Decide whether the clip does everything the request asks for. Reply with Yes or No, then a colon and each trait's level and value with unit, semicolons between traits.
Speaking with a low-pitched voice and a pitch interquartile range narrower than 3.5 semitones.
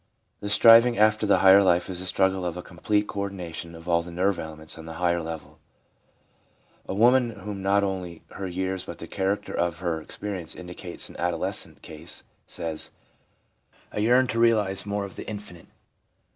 Yes: very low, 95 Hz; average, 3.1 semitones